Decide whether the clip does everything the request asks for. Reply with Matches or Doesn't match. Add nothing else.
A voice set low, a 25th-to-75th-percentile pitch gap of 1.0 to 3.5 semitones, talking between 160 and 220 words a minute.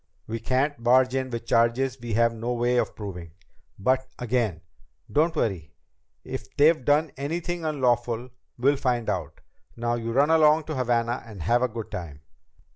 Matches